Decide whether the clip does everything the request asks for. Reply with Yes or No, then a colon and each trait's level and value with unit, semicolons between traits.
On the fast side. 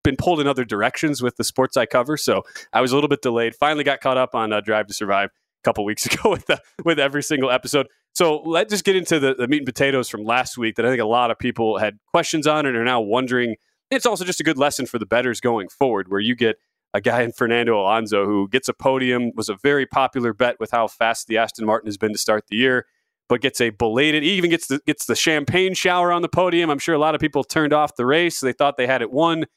Yes: fast, 270 wpm